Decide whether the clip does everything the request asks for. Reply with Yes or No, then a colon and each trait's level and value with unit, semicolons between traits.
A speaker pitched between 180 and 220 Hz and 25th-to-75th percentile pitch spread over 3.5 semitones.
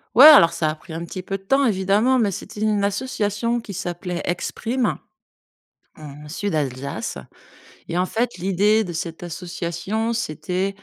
Yes: high, 190 Hz; average, 4.4 semitones